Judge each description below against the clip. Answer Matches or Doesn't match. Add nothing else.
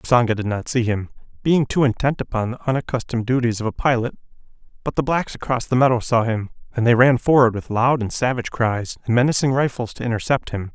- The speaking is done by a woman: Doesn't match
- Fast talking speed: Matches